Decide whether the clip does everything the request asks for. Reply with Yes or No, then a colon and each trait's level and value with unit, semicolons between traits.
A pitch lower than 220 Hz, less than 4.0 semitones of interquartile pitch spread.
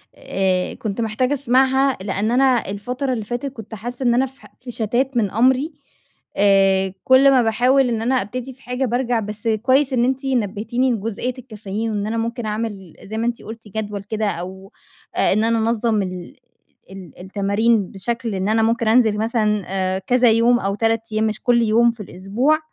No: high, 225 Hz; average, 3.2 semitones